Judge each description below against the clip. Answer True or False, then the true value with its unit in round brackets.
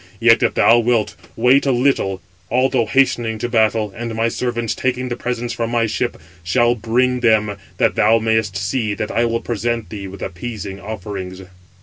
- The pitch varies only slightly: True (2.2 semitones)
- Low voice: True (115 Hz)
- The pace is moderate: True (180 wpm)